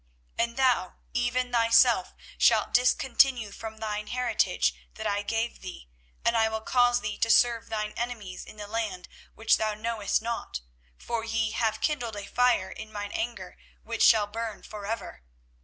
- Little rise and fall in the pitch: Yes, narrow, 2.0 semitones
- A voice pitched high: Yes, high, 225 Hz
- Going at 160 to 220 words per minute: Yes, average, 170 wpm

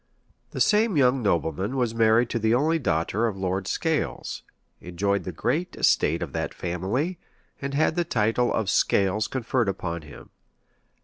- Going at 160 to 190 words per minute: Yes, average, 165 wpm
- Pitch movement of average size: No, wide, 6.1 semitones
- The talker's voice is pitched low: Yes, low, 110 Hz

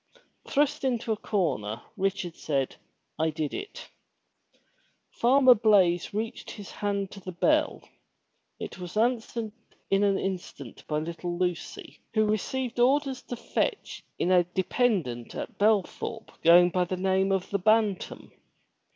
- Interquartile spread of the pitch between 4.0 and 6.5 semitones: Yes, average, 4.3 semitones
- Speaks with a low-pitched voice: No, high, 195 Hz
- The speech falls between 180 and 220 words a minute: No, slow, 135 wpm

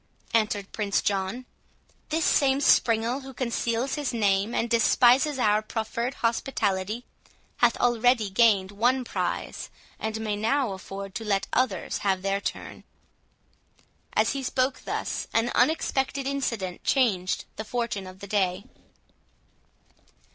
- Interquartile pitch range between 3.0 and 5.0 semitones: Yes, average, 4.1 semitones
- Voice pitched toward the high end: Yes, high, 225 Hz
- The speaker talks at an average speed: No, slow, 125 wpm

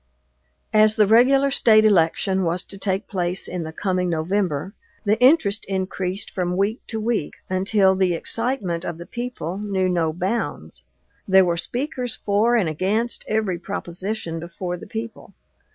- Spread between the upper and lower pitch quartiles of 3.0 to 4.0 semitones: Yes, average, 3.7 semitones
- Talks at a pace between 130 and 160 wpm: Yes, average, 150 wpm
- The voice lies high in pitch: Yes, high, 195 Hz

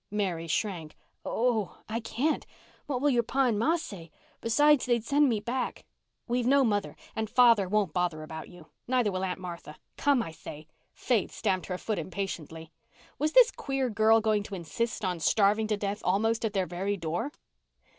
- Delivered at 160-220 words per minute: Yes, average, 175 wpm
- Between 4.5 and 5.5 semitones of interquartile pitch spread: Yes, average, 4.8 semitones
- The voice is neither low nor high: No, high, 210 Hz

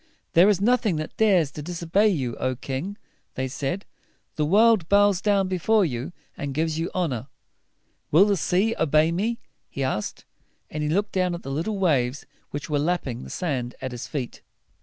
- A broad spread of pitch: Yes, wide, 6.1 semitones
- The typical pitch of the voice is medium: Yes, medium, 165 Hz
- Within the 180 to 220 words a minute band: Yes, average, 185 wpm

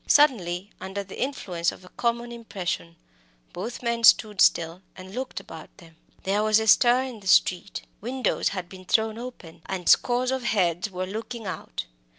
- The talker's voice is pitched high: Yes, high, 205 Hz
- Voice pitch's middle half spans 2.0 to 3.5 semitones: No, average, 4.5 semitones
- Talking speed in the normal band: Yes, average, 170 wpm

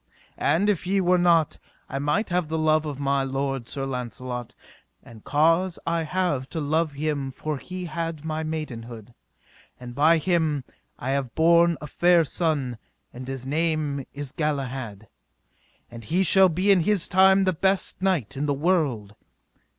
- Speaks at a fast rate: No, average, 165 wpm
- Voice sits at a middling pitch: Yes, medium, 155 Hz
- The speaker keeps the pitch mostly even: No, average, 4.1 semitones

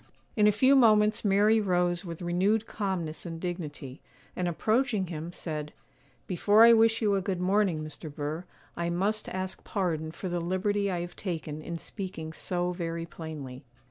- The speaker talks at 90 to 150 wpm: No, average, 170 wpm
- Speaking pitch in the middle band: Yes, medium, 180 Hz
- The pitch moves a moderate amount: Yes, average, 3.7 semitones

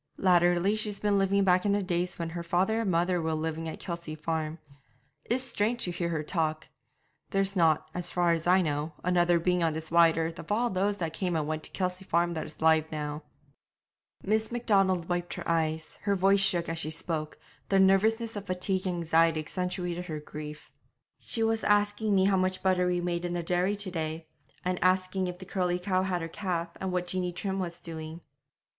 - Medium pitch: Yes, medium, 180 Hz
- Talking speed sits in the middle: No, fast, 210 wpm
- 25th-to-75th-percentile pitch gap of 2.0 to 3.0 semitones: Yes, narrow, 2.6 semitones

